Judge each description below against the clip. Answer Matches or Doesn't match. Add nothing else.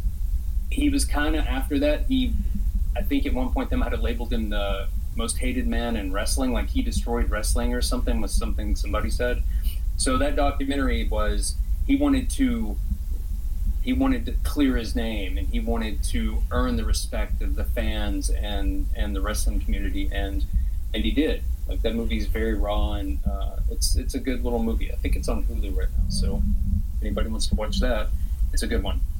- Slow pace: Doesn't match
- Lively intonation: Matches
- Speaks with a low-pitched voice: Matches